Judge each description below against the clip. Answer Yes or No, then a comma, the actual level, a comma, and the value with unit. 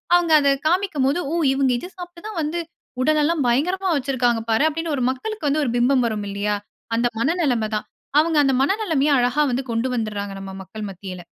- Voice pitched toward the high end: Yes, very high, 275 Hz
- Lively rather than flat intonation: Yes, wide, 5.7 semitones